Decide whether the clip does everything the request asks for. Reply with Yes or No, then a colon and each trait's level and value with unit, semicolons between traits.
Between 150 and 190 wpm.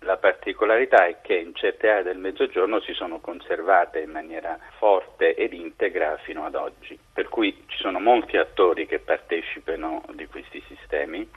Yes: average, 165 wpm